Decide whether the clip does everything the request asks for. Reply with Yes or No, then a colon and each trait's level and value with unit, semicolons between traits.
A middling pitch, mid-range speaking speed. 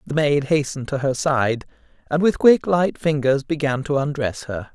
Yes: medium, 145 Hz; average, 190 wpm